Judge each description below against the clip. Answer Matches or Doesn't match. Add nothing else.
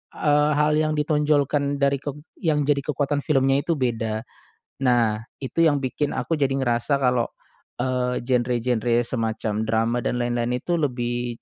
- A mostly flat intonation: Doesn't match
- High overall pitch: Doesn't match